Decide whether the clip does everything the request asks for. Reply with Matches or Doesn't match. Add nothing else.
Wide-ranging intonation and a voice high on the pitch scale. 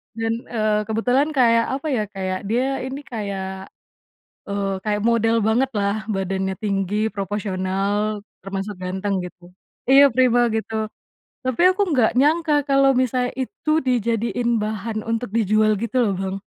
Doesn't match